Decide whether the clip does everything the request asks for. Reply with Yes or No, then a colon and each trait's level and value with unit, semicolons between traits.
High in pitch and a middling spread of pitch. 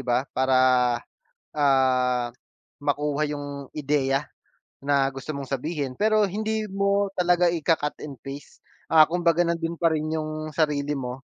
No: medium, 150 Hz; average, 3.6 semitones